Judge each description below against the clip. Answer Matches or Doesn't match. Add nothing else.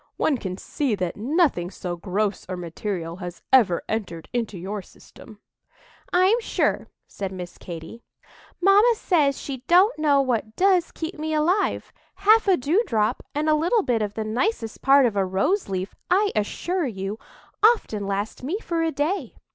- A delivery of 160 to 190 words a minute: Matches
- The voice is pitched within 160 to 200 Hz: Doesn't match